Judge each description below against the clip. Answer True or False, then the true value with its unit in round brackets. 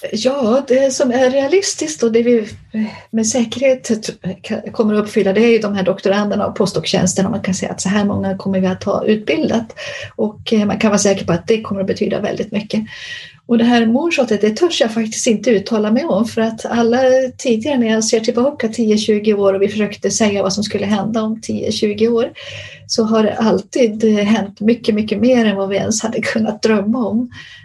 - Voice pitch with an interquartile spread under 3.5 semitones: True (2.6 semitones)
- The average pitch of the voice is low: False (220 Hz)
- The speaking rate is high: True (205 wpm)